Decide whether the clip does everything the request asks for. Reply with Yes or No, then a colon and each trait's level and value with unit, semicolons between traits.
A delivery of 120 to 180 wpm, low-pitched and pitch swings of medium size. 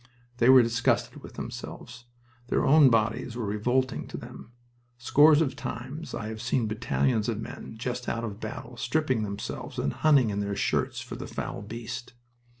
Yes: average, 170 wpm; low, 120 Hz; average, 3.0 semitones